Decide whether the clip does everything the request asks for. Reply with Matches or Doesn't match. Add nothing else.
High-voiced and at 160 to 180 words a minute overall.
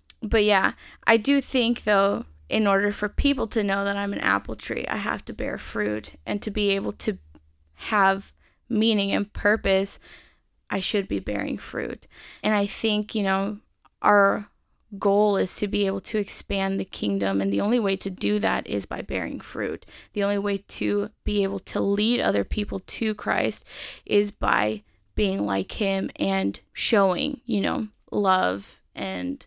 Matches